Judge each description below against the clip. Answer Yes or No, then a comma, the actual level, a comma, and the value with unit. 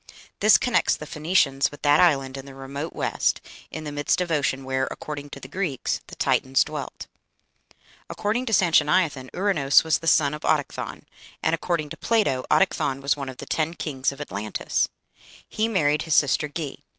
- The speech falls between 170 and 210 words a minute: Yes, average, 180 wpm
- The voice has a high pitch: No, medium, 150 Hz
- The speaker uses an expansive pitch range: No, average, 3.6 semitones